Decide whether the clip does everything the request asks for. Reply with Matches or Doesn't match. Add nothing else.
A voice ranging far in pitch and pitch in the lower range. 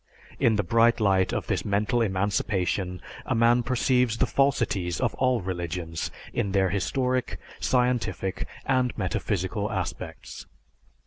Doesn't match